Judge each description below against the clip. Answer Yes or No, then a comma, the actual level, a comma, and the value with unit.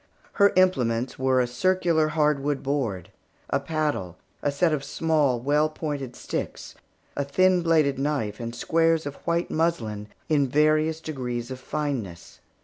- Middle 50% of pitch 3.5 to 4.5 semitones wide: Yes, average, 4.1 semitones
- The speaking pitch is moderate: Yes, medium, 145 Hz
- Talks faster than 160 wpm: No, average, 140 wpm